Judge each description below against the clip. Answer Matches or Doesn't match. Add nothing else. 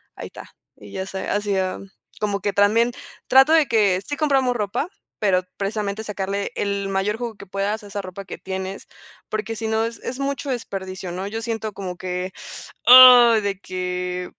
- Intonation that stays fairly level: Doesn't match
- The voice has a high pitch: Matches